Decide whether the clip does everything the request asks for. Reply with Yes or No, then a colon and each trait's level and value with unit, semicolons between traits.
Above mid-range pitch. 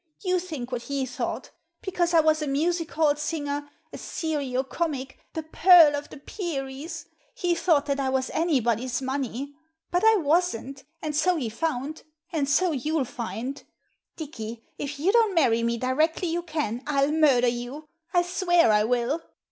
Yes: very high, 290 Hz